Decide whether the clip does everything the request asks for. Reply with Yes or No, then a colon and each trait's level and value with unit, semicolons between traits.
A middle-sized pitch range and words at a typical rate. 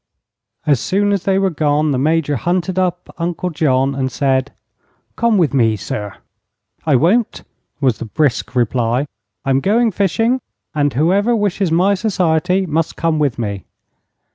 No: wide, 5.9 semitones; average, 150 wpm